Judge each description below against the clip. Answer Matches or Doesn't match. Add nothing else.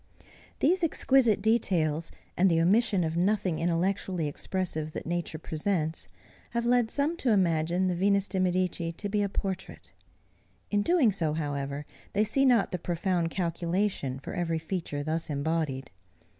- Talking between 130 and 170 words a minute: Matches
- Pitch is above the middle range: Doesn't match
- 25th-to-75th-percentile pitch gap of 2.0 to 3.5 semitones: Doesn't match